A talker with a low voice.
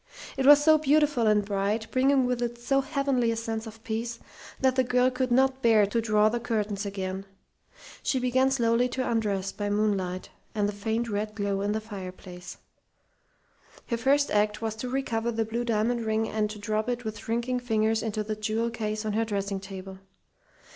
No: high, 225 Hz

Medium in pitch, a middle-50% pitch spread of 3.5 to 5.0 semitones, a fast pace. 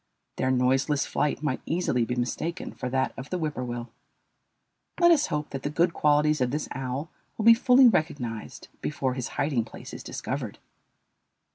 No: medium, 145 Hz; average, 4.1 semitones; average, 165 wpm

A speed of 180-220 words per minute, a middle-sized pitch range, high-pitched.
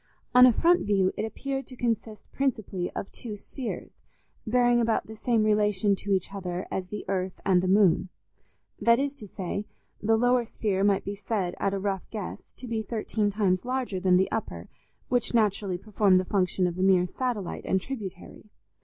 Yes: average, 190 wpm; average, 3.5 semitones; high, 205 Hz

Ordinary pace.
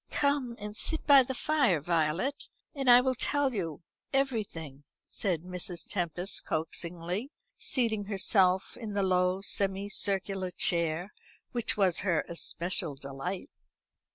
No: slow, 125 wpm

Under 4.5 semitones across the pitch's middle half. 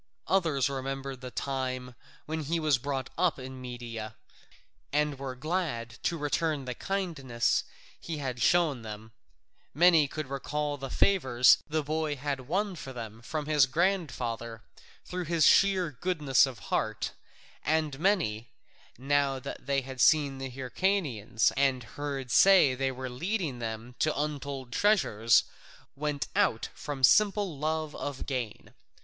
Yes: average, 3.8 semitones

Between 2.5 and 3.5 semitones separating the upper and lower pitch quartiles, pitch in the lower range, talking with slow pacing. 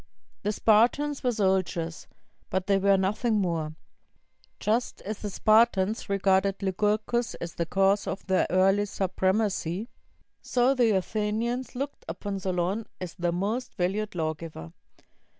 No: average, 2.8 semitones; high, 195 Hz; slow, 130 wpm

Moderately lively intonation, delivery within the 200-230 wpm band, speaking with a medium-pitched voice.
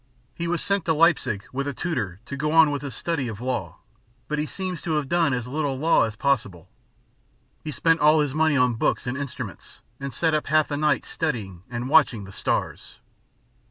Yes: average, 4.3 semitones; fast, 205 wpm; medium, 145 Hz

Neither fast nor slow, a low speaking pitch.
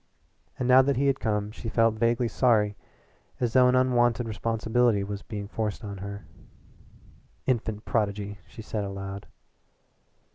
Yes: average, 145 wpm; low, 110 Hz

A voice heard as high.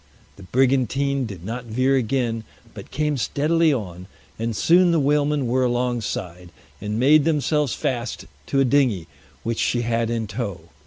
No: low, 125 Hz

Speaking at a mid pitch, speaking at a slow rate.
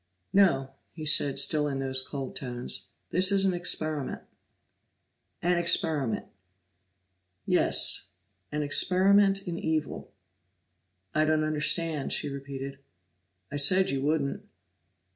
Yes: medium, 155 Hz; slow, 110 wpm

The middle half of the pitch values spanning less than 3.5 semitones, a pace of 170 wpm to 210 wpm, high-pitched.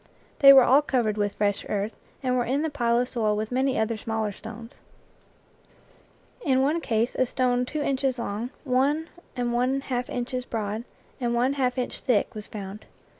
Yes: average, 3.1 semitones; average, 180 wpm; high, 245 Hz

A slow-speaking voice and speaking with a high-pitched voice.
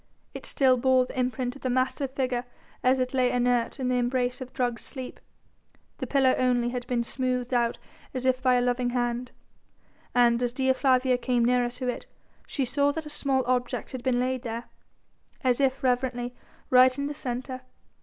No: average, 190 wpm; very high, 255 Hz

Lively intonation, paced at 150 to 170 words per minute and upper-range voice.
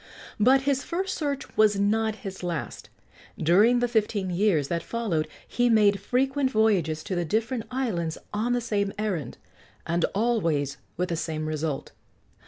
Yes: wide, 6.0 semitones; average, 155 wpm; high, 210 Hz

